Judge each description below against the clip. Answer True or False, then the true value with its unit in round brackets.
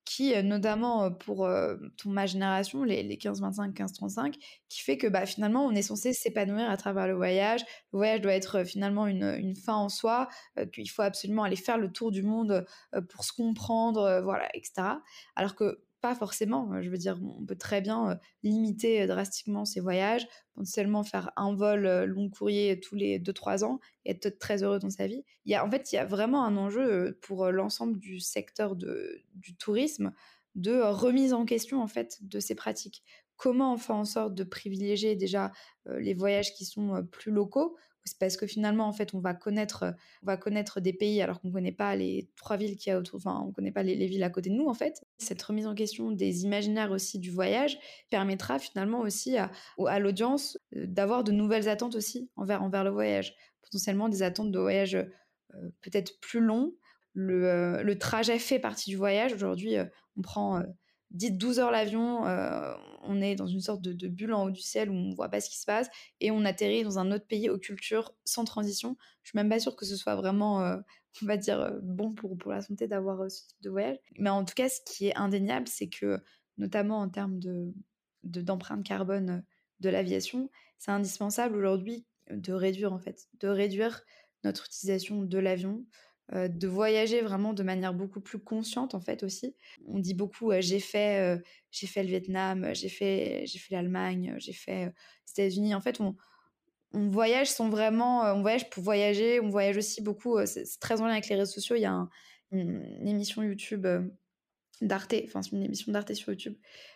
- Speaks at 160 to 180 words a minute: False (210 wpm)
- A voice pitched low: False (200 Hz)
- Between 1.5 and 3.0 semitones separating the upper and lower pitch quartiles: True (2.6 semitones)